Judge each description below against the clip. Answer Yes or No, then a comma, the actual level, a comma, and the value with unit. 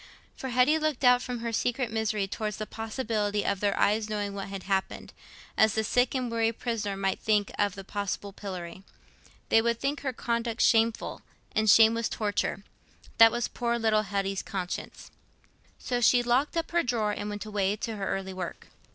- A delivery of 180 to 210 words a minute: Yes, average, 185 wpm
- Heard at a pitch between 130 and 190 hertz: No, high, 220 Hz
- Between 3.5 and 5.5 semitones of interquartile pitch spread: No, average, 2.8 semitones